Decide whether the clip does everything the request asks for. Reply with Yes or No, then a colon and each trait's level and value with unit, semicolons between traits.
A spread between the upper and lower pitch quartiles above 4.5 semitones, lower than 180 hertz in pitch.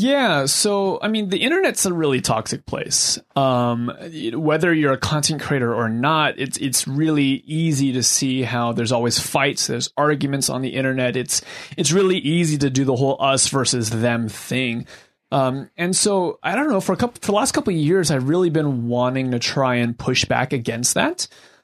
Yes: wide, 5.5 semitones; medium, 140 Hz